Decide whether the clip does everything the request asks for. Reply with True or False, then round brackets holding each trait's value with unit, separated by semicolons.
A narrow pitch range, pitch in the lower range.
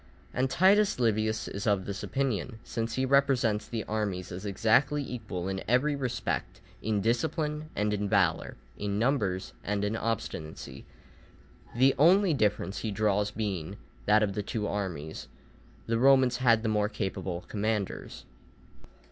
False (4.1 semitones; 110 Hz)